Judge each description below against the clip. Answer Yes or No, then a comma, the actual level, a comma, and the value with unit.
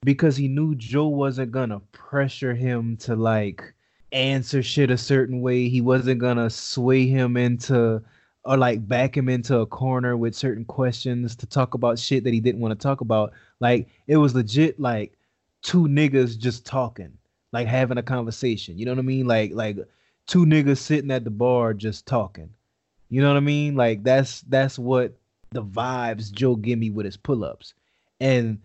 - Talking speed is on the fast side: No, average, 180 wpm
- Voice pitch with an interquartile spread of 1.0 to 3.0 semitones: Yes, narrow, 2.5 semitones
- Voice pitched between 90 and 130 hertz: Yes, low, 125 Hz